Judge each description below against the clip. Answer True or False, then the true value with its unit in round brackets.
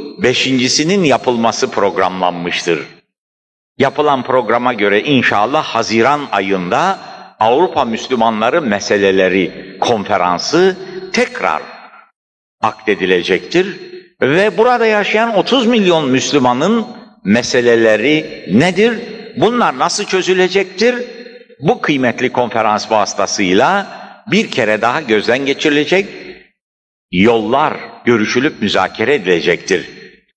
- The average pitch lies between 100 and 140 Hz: True (135 Hz)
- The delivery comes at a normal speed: False (75 wpm)